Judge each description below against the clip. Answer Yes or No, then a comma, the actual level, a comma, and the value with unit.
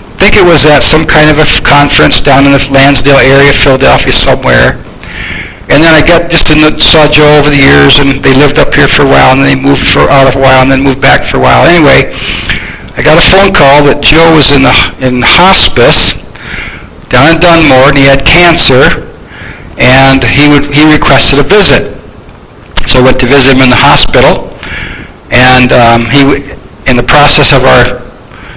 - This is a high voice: No, medium, 140 Hz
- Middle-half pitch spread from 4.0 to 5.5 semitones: No, average, 2.7 semitones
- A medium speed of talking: No, fast, 210 wpm